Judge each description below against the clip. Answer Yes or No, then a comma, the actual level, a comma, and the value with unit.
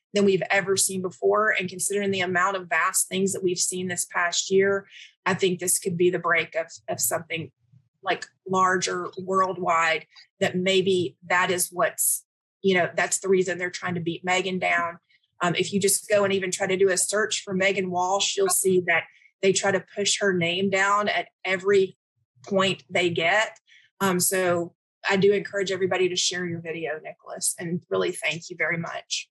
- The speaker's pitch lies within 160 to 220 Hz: Yes, medium, 185 Hz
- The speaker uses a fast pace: No, average, 190 wpm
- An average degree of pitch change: No, narrow, 1.8 semitones